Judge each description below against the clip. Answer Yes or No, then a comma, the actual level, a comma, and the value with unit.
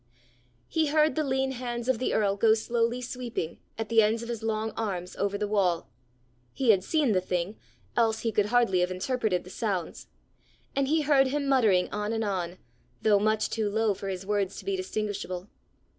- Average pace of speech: Yes, average, 195 wpm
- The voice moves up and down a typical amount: Yes, average, 3.9 semitones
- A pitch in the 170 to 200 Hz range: No, high, 220 Hz